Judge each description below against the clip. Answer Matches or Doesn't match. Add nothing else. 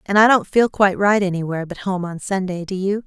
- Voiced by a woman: Matches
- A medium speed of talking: Doesn't match